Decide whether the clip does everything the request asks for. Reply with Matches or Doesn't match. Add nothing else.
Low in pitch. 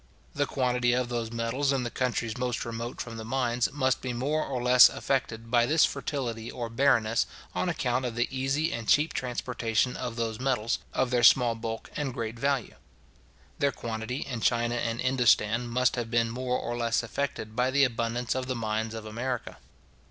Matches